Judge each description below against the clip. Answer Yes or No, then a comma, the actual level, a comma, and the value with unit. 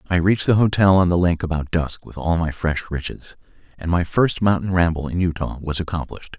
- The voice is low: Yes, very low, 85 Hz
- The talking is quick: Yes, fast, 215 wpm